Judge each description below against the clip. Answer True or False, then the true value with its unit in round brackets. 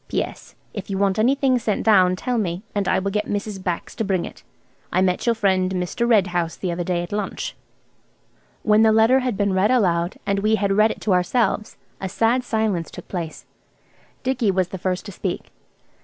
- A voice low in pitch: False (200 Hz)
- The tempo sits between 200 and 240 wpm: True (205 wpm)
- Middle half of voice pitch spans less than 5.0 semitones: True (3.2 semitones)